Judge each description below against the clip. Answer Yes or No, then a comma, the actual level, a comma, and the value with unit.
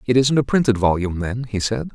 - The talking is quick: Yes, fast, 245 wpm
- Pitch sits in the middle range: No, low, 115 Hz